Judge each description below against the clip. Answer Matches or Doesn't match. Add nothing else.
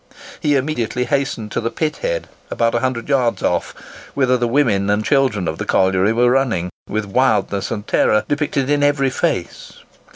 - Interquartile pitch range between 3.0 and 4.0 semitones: Doesn't match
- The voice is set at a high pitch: Doesn't match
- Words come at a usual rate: Matches